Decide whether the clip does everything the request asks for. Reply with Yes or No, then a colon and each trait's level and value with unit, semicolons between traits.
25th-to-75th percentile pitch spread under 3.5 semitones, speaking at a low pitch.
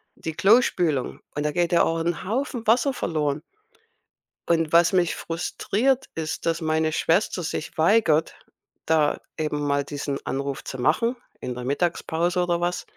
No: average, 2.9 semitones; medium, 165 Hz